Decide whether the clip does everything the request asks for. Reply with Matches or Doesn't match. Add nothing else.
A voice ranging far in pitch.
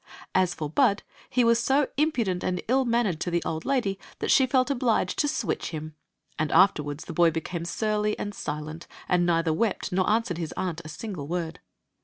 Matches